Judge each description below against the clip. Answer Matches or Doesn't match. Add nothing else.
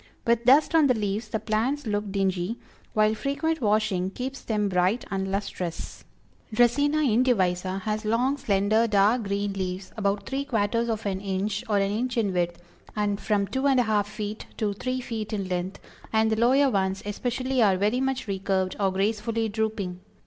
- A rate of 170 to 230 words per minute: Matches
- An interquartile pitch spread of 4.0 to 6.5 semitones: Doesn't match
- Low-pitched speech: Doesn't match